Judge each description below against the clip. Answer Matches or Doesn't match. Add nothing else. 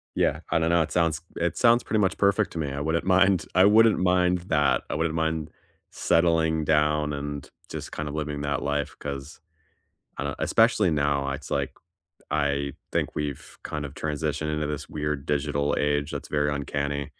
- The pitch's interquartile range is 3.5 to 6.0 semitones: Doesn't match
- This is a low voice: Matches